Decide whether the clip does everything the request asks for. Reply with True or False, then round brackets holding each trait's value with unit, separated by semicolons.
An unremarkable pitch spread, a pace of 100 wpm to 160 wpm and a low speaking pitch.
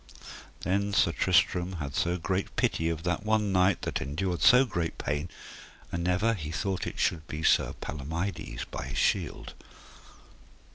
True (3.3 semitones; 155 wpm; 90 Hz)